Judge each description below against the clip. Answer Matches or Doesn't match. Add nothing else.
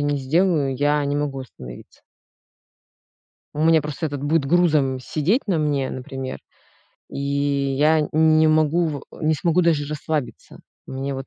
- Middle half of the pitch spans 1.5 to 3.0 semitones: Matches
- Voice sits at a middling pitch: Matches